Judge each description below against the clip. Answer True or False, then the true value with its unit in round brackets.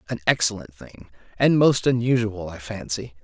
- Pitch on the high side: False (110 Hz)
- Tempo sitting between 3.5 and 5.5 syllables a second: True (5.0 syllables/s)